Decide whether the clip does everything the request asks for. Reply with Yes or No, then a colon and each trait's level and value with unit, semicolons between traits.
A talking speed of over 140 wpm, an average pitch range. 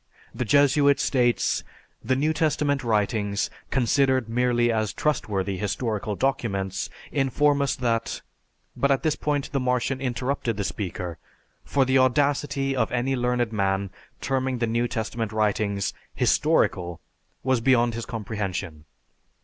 No: slow, 135 wpm; average, 4.1 semitones